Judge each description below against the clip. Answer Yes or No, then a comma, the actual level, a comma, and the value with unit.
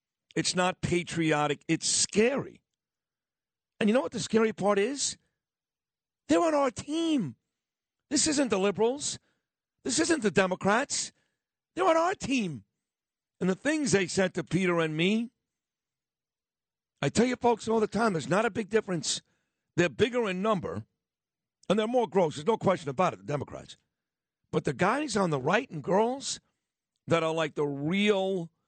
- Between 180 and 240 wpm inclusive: No, average, 165 wpm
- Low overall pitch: No, high, 200 Hz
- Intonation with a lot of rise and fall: Yes, wide, 5.7 semitones